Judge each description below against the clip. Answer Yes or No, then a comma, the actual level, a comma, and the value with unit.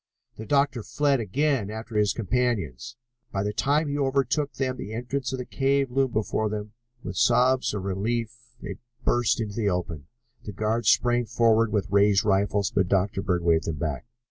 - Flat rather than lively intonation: No, average, 4.1 semitones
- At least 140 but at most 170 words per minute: No, average, 185 wpm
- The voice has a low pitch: Yes, low, 110 Hz